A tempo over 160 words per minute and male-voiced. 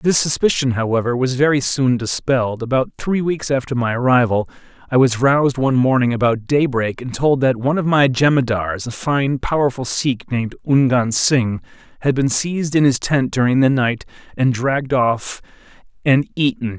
Yes: average, 170 wpm; male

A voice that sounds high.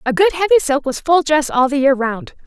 Yes: very high, 295 Hz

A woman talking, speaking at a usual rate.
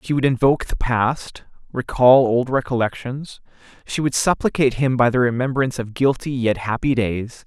No: male; average, 160 wpm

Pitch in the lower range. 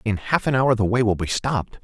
Yes: low, 110 Hz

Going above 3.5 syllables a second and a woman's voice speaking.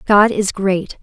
No: 3.3 syllables/s; female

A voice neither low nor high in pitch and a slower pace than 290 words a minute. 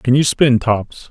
No: low, 125 Hz; fast, 215 wpm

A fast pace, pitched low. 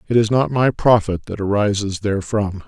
No: average, 180 wpm; low, 105 Hz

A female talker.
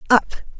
Yes: female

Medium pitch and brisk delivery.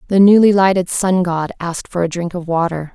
Yes: medium, 180 Hz; fast, 225 wpm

